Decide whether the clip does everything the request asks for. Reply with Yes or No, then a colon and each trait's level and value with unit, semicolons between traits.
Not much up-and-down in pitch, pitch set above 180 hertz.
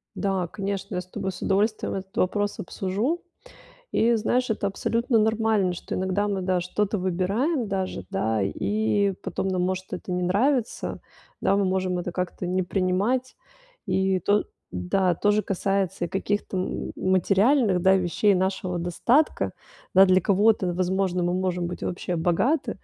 Yes: narrow, 2.3 semitones; high, 190 Hz